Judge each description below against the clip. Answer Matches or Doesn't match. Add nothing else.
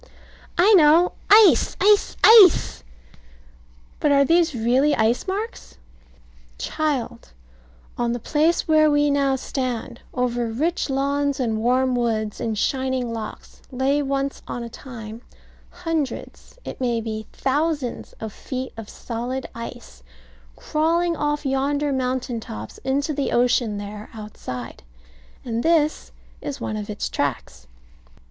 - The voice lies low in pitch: Doesn't match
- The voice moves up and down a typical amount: Matches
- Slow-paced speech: Matches